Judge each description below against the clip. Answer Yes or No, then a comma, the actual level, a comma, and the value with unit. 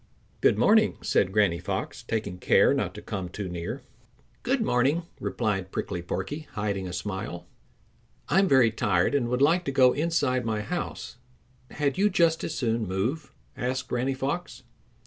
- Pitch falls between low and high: No, low, 125 Hz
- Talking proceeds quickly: No, average, 160 wpm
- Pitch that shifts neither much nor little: No, wide, 6.6 semitones